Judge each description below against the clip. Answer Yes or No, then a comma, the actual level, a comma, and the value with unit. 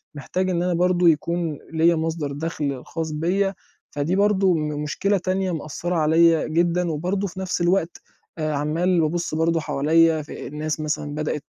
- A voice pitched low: No, medium, 165 Hz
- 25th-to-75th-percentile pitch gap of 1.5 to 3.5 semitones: Yes, average, 2.7 semitones